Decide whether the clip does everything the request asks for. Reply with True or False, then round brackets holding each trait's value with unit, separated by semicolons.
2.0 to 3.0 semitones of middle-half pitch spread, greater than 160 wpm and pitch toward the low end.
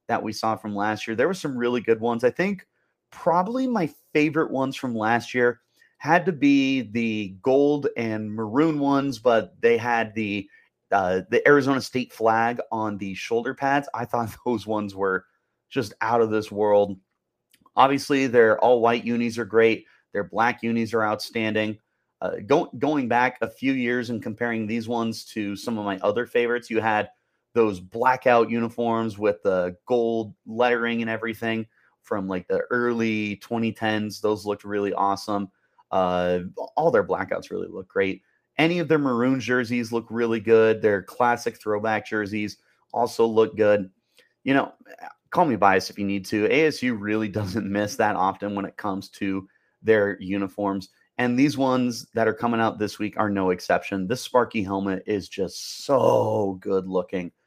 True (2.7 semitones; 170 wpm; 115 Hz)